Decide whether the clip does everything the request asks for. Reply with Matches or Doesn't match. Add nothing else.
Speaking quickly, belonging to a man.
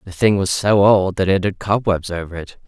Matches